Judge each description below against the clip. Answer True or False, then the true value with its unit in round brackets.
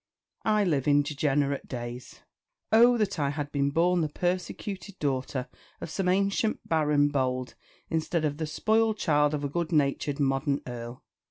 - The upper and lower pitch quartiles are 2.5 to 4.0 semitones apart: False (4.4 semitones)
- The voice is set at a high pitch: False (150 Hz)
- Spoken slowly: False (160 wpm)